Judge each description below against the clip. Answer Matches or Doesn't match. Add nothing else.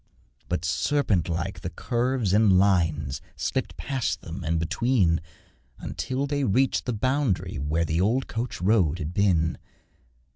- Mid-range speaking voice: Doesn't match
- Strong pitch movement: Matches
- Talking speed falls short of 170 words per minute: Matches